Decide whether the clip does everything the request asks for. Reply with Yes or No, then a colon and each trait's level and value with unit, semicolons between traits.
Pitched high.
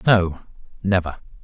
No: very low, 90 Hz